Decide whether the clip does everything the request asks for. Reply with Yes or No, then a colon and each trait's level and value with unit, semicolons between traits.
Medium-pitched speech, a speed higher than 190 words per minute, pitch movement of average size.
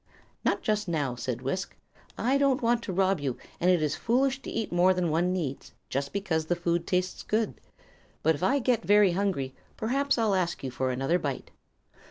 No: medium, 180 Hz; average, 200 wpm; wide, 5.9 semitones